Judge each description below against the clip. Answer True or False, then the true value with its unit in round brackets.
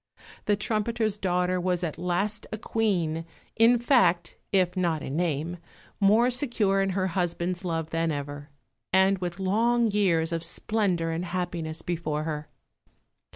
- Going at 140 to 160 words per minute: True (145 wpm)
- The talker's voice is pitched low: False (180 Hz)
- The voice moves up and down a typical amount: True (3.8 semitones)